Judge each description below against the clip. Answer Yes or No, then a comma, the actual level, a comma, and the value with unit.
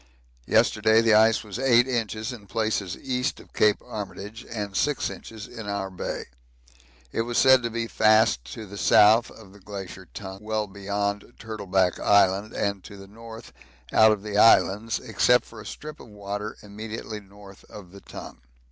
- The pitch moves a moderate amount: No, narrow, 2.0 semitones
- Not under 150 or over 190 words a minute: Yes, average, 175 wpm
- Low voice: Yes, low, 105 Hz